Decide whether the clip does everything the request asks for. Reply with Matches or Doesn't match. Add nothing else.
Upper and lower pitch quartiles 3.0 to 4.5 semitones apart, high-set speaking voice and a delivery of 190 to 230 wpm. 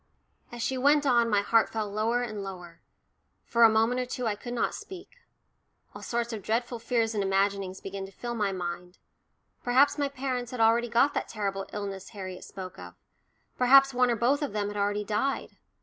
Matches